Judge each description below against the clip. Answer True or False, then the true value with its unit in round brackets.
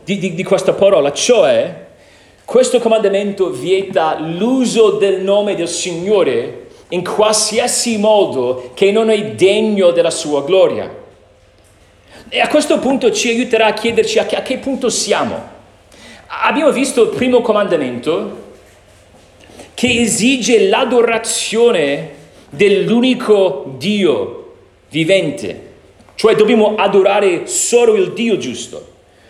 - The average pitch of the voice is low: False (215 Hz)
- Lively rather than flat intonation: False (4.7 semitones)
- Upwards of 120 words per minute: False (115 wpm)